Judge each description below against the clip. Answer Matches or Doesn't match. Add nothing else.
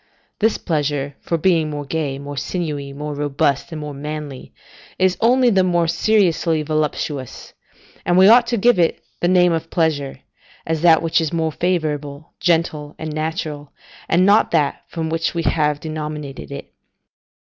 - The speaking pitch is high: Doesn't match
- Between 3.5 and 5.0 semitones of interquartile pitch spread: Doesn't match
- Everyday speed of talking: Matches